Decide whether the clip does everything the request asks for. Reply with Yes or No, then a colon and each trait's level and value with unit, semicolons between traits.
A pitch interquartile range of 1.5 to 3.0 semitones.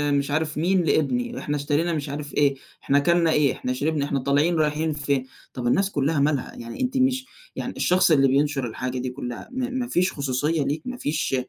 No: average, 3.7 semitones